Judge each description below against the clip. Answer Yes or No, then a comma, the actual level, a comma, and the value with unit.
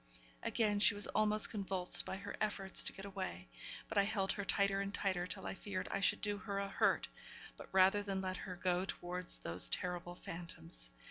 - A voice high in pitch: Yes, high, 195 Hz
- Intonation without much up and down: Yes, narrow, 2.0 semitones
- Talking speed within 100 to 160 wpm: No, fast, 205 wpm